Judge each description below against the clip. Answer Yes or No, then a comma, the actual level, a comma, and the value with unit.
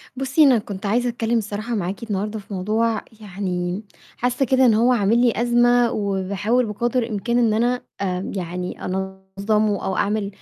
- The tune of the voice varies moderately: Yes, average, 3.5 semitones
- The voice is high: Yes, high, 215 Hz